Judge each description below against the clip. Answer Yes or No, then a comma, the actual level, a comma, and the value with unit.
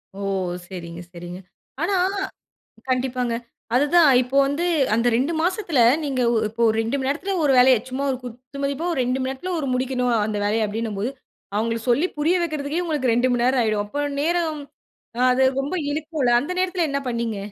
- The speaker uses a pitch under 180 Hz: No, very high, 260 Hz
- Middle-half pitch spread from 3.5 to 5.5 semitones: Yes, average, 4.3 semitones